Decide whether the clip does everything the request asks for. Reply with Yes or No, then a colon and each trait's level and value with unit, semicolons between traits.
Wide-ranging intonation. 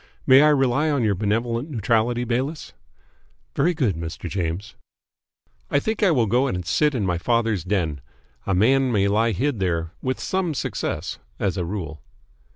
Yes: wide, 6.2 semitones